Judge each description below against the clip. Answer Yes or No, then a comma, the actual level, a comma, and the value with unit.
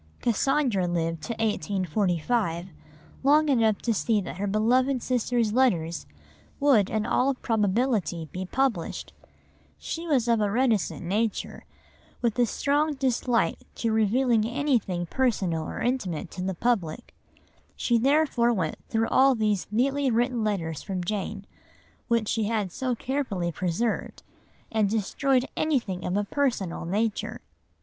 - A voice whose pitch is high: Yes, high, 225 Hz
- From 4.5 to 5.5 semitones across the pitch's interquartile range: Yes, average, 4.9 semitones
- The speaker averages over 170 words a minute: No, slow, 135 wpm